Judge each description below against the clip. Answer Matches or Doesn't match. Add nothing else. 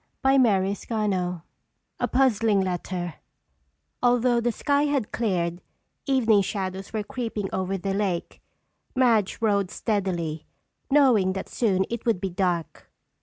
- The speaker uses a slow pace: Matches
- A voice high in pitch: Matches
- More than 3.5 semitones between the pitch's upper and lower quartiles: Matches